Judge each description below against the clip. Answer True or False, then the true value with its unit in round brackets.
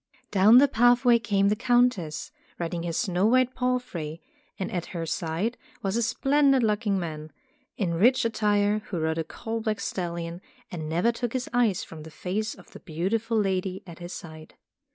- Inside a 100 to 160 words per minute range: False (175 wpm)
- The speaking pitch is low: False (200 Hz)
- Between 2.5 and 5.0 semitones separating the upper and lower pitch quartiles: False (5.4 semitones)